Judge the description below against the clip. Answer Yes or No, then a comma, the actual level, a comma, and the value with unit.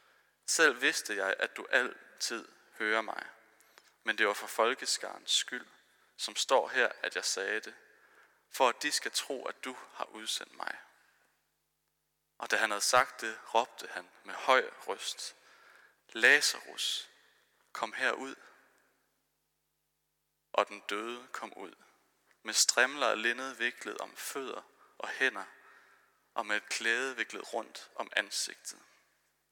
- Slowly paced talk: Yes, slow, 135 wpm